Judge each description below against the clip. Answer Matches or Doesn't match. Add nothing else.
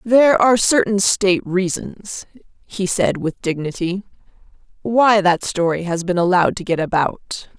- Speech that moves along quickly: Doesn't match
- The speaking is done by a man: Doesn't match